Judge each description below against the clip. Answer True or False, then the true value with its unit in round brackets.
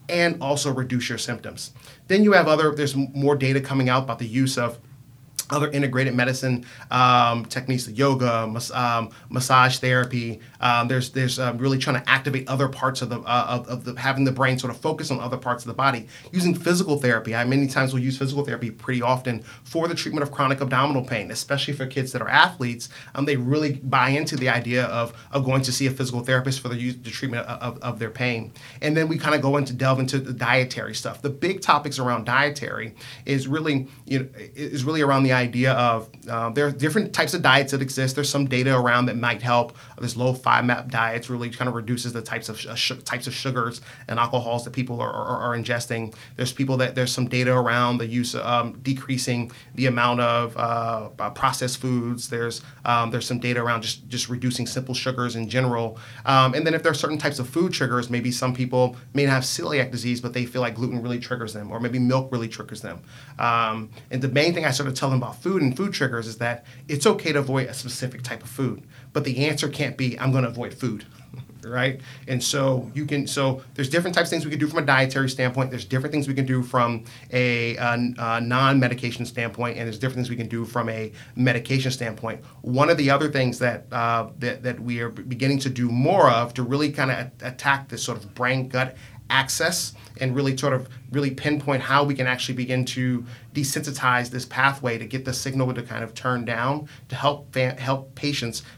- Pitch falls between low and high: False (125 Hz)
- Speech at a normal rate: False (225 wpm)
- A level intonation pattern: True (2.1 semitones)